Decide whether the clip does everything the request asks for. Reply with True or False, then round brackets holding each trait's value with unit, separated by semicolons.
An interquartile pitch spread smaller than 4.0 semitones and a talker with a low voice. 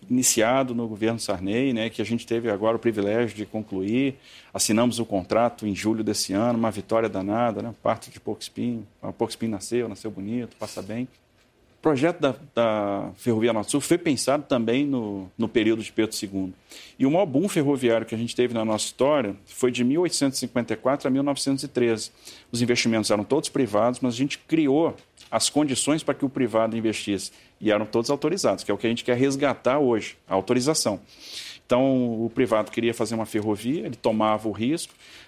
True (2.8 semitones; 115 Hz)